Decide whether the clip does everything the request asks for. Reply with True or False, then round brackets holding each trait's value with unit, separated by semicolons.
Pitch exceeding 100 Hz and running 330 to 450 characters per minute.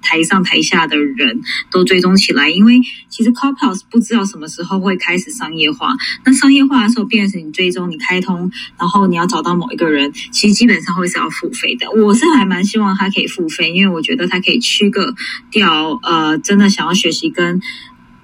True (190 Hz; 335 characters per minute)